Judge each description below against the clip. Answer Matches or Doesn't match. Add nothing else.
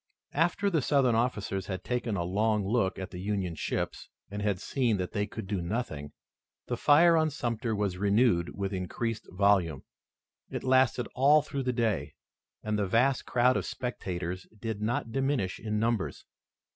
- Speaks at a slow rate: Doesn't match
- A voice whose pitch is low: Matches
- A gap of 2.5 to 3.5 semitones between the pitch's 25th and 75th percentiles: Doesn't match